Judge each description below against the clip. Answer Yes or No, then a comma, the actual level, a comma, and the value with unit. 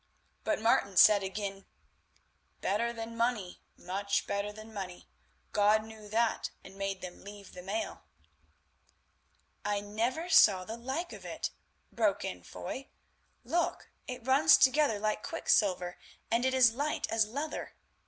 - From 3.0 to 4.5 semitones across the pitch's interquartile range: Yes, average, 3.6 semitones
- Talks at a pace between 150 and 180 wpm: No, slow, 135 wpm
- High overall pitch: Yes, high, 215 Hz